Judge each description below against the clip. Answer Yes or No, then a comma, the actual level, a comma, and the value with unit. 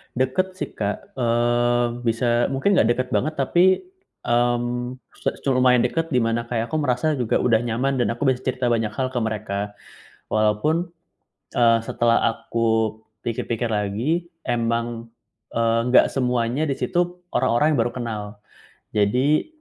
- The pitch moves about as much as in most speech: No, narrow, 2.3 semitones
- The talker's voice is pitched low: Yes, low, 120 Hz